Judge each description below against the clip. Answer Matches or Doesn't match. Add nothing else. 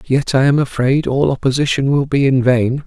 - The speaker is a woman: Doesn't match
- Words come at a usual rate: Doesn't match